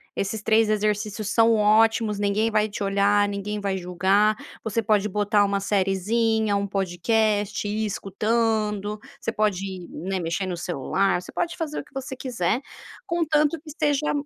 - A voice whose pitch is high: Yes, high, 210 Hz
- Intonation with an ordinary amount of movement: No, narrow, 2.2 semitones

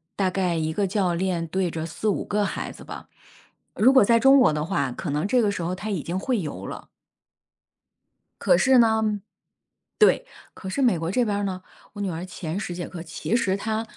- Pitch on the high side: Yes, high, 195 Hz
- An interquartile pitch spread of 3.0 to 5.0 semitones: Yes, average, 4.3 semitones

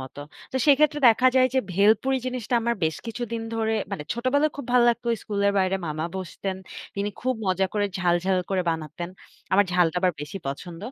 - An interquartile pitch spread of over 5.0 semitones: Yes, wide, 5.4 semitones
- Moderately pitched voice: No, high, 205 Hz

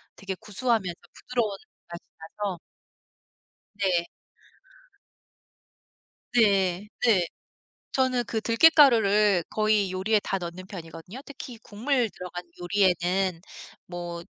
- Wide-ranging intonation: No, average, 4.0 semitones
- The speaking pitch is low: No, high, 200 Hz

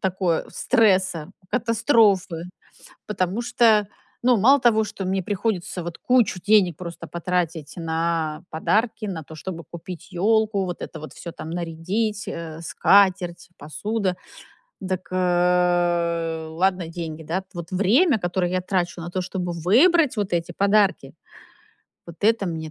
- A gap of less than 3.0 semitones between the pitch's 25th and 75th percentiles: No, average, 3.5 semitones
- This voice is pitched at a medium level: Yes, medium, 180 Hz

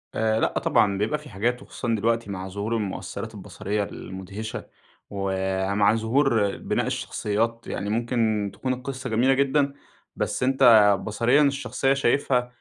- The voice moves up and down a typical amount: Yes, average, 3.9 semitones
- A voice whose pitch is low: Yes, low, 115 Hz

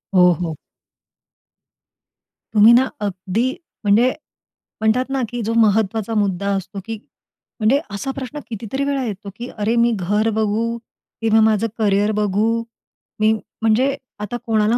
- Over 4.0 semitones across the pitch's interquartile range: No, narrow, 2.5 semitones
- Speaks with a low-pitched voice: No, high, 220 Hz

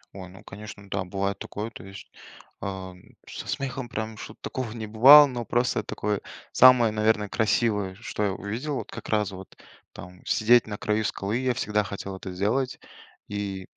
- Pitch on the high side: No, low, 105 Hz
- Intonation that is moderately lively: Yes, average, 3.2 semitones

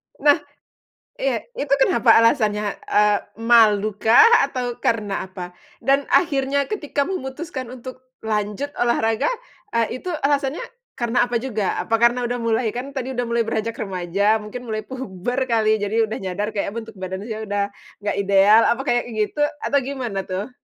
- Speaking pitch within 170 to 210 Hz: No, high, 230 Hz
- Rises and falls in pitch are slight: No, average, 3.9 semitones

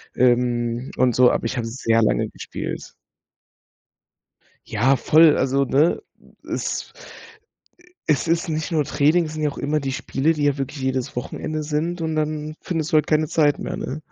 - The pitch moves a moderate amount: Yes, average, 3.3 semitones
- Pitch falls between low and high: Yes, medium, 145 Hz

